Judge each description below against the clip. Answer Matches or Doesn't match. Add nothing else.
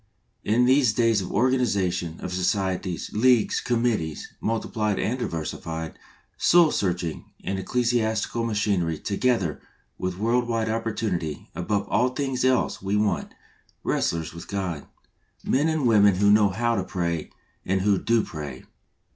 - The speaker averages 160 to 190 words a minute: Doesn't match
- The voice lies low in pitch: Matches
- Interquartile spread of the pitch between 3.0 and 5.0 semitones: Matches